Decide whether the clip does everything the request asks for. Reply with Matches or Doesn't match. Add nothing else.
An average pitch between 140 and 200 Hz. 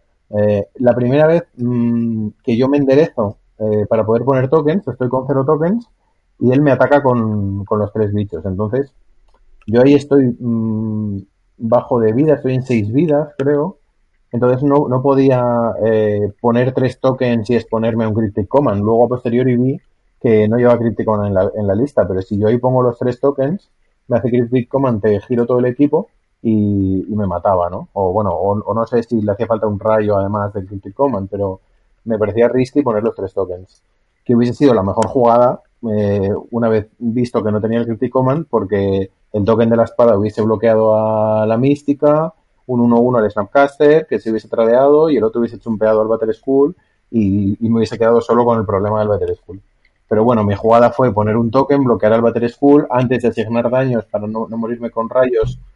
Doesn't match